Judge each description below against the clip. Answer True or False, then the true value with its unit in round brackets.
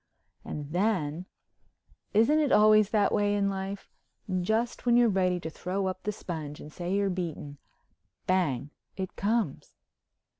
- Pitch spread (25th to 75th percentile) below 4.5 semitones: True (3.4 semitones)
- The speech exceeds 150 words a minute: False (135 wpm)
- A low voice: False (190 Hz)